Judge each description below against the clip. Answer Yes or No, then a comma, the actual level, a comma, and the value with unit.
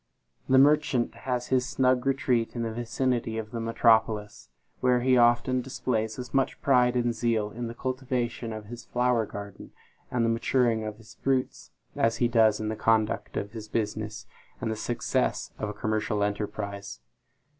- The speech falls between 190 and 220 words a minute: No, average, 170 wpm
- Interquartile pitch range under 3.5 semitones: Yes, narrow, 2.4 semitones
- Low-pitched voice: Yes, low, 115 Hz